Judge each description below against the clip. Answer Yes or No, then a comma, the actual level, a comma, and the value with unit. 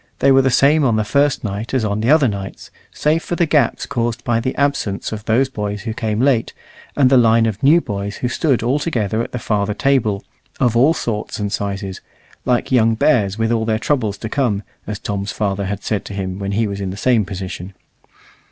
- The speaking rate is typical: No, fast, 225 wpm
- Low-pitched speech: Yes, low, 110 Hz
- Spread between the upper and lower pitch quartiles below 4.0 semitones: No, average, 4.3 semitones